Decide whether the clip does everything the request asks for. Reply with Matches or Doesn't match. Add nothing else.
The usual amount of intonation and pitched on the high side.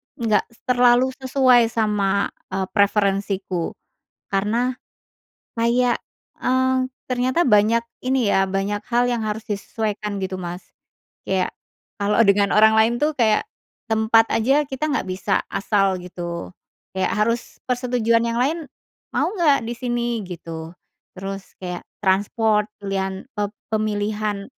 Matches